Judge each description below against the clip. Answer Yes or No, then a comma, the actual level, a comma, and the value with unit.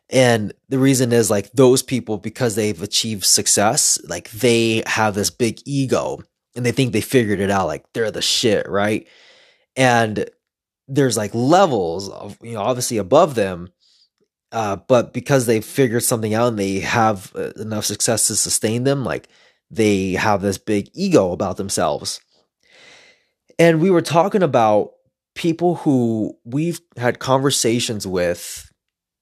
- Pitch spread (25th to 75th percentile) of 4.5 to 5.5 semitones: Yes, average, 4.8 semitones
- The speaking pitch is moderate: No, low, 120 Hz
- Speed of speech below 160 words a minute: Yes, average, 150 wpm